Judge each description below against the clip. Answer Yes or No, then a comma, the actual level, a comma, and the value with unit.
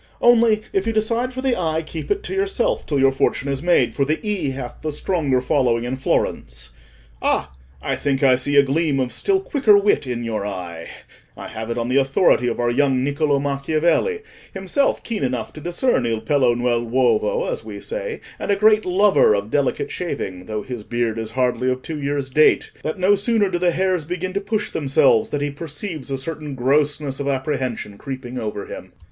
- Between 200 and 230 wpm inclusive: Yes, fast, 205 wpm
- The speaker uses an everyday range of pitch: No, wide, 6.9 semitones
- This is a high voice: No, medium, 145 Hz